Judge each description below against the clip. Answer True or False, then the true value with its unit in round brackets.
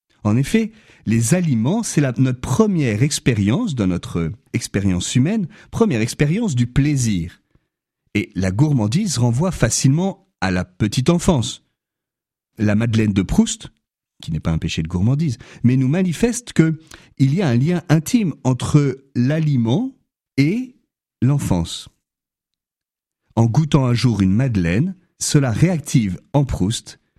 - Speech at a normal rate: False (130 wpm)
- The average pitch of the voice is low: True (130 Hz)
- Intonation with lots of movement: True (6.6 semitones)